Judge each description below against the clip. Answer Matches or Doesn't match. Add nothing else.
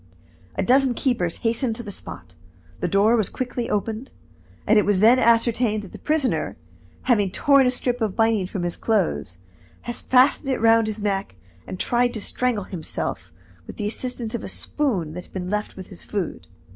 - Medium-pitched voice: Doesn't match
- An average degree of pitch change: Matches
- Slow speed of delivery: Doesn't match